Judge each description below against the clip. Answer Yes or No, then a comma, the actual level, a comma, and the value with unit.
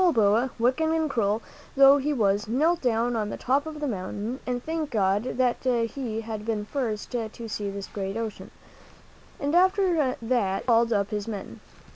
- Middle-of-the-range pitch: No, high, 235 Hz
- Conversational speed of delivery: Yes, average, 185 wpm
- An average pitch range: Yes, average, 4.7 semitones